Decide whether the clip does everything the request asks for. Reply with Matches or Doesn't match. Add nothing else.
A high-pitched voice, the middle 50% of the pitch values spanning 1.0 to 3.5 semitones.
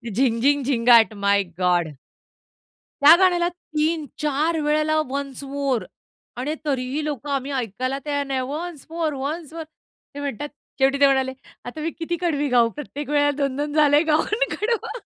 Matches